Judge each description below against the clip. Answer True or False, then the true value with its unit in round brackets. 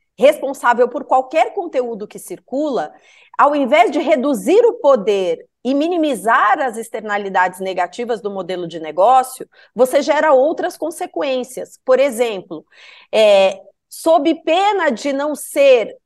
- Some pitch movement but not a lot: False (6.5 semitones)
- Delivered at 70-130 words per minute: True (125 wpm)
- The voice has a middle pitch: False (270 Hz)